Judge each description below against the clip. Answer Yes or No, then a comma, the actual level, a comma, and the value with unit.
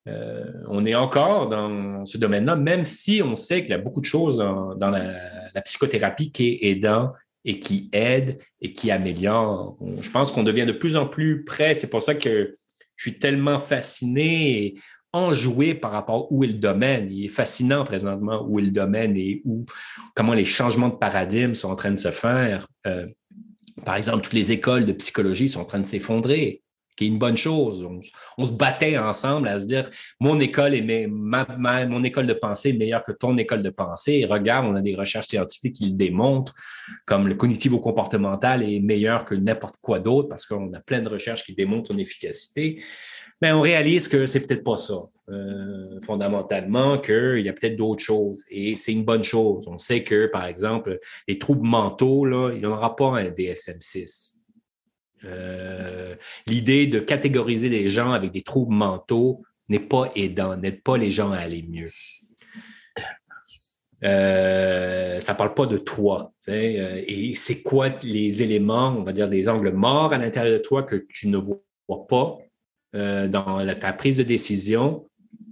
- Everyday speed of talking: Yes, average, 190 wpm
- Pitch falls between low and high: No, low, 115 Hz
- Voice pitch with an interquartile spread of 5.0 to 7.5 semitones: Yes, wide, 5.4 semitones